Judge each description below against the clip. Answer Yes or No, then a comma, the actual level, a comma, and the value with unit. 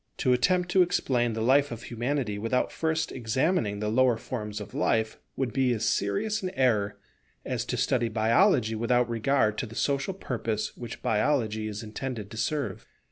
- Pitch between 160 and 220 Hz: No, low, 120 Hz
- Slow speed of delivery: No, average, 175 wpm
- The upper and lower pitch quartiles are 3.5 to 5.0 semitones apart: Yes, average, 4.0 semitones